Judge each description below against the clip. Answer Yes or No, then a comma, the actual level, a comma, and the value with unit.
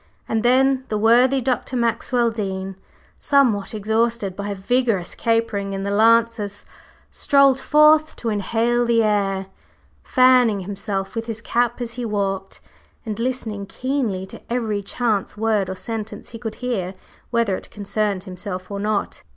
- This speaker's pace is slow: No, average, 145 wpm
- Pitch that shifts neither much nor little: Yes, average, 3.3 semitones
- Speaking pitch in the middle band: No, high, 220 Hz